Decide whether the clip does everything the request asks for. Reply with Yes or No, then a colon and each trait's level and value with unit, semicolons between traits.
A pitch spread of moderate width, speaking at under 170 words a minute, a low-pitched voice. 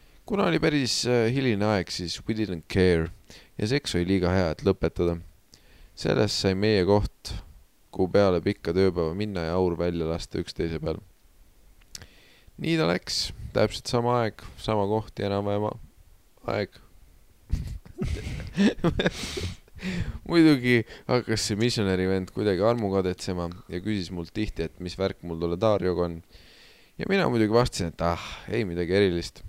Yes: average, 4.1 semitones; average, 140 wpm; low, 100 Hz